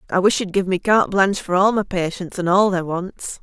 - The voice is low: No, high, 190 Hz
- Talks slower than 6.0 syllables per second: Yes, 5.6 syllables/s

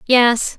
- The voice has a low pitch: No, high, 240 Hz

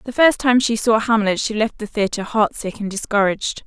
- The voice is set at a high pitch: Yes, high, 220 Hz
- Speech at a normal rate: No, fast, 215 wpm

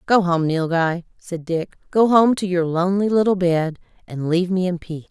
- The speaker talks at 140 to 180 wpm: No, average, 200 wpm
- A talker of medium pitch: Yes, medium, 180 Hz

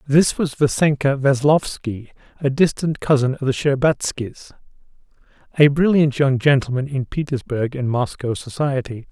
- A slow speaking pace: Yes, slow, 125 wpm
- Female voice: No, male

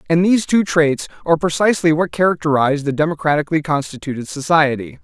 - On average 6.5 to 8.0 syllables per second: Yes, 6.7 syllables/s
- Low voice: No, medium, 160 Hz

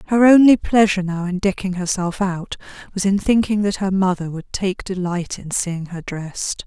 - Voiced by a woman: Yes, female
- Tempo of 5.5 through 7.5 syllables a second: No, 4.9 syllables/s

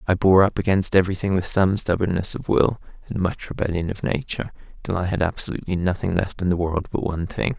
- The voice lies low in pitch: Yes, very low, 90 Hz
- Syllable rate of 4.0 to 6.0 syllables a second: No, 6.3 syllables/s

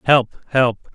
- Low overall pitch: Yes, low, 125 Hz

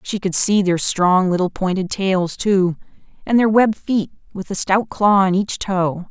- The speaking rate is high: No, average, 195 wpm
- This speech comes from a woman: Yes, female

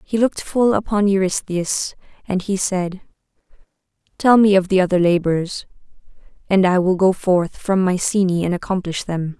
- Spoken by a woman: Yes, female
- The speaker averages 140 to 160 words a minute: Yes, average, 155 wpm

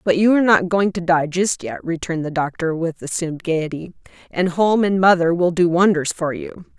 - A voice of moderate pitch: Yes, medium, 175 Hz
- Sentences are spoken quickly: Yes, fast, 210 wpm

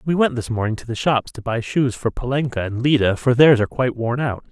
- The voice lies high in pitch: No, low, 125 Hz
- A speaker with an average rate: No, fast, 265 wpm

